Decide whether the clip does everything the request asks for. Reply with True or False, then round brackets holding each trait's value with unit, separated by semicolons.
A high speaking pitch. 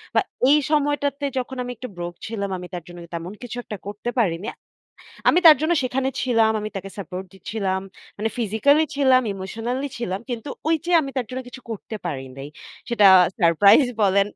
True (225 Hz)